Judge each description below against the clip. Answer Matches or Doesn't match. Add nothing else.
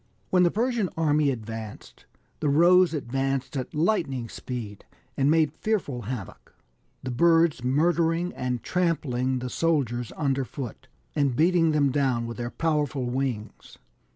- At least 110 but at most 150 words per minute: Matches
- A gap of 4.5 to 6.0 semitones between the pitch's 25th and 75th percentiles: Matches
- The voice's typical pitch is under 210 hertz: Matches